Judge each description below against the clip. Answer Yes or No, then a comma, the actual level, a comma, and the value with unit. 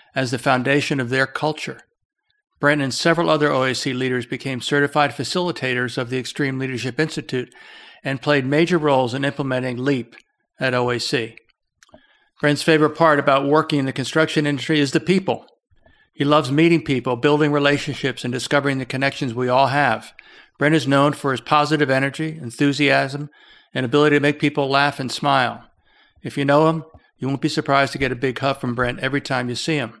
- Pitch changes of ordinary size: No, narrow, 2.3 semitones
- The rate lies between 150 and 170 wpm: No, average, 180 wpm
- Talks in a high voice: No, medium, 140 Hz